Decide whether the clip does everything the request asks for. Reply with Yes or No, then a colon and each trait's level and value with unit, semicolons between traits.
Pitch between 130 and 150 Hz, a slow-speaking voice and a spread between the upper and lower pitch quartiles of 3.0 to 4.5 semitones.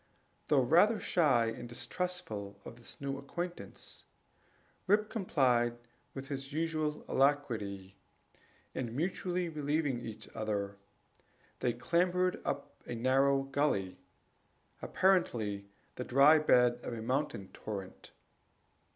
No: low, 135 Hz; slow, 110 wpm; average, 5.1 semitones